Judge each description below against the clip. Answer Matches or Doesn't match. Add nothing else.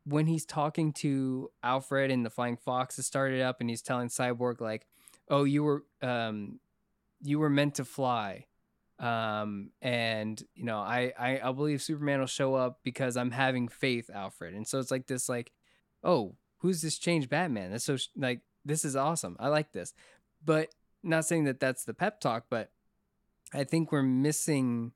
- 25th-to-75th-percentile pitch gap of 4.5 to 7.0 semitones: Doesn't match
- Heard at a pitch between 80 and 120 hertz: Doesn't match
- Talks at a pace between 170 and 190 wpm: Matches